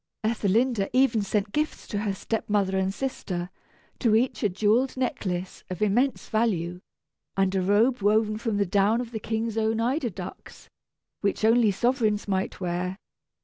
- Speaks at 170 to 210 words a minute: No, average, 160 wpm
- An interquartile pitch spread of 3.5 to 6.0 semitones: No, average, 3.1 semitones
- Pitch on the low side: No, high, 215 Hz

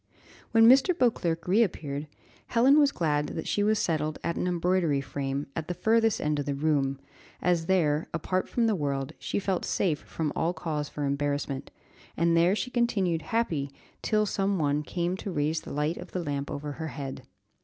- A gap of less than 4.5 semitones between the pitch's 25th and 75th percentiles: No, average, 4.8 semitones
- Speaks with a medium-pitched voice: Yes, medium, 165 Hz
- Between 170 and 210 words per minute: Yes, average, 185 wpm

